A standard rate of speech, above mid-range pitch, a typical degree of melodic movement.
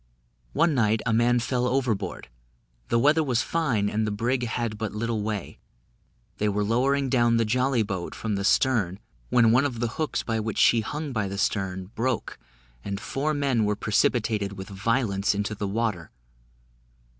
No: average, 175 wpm; low, 115 Hz; average, 3.4 semitones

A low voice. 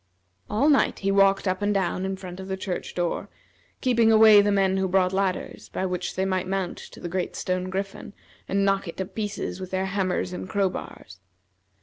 No: high, 190 Hz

